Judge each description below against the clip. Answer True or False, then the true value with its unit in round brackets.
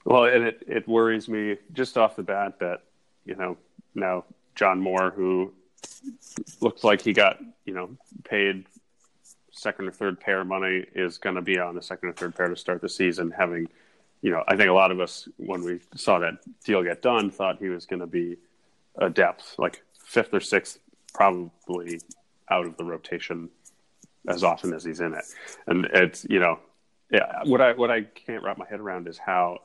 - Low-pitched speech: True (95 Hz)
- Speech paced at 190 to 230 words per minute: True (200 wpm)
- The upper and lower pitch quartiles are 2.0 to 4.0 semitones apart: True (2.7 semitones)